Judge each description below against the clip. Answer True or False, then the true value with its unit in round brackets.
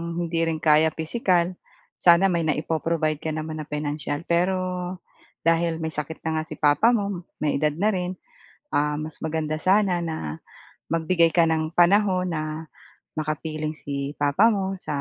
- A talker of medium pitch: True (160 Hz)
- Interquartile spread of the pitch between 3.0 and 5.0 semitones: False (2.4 semitones)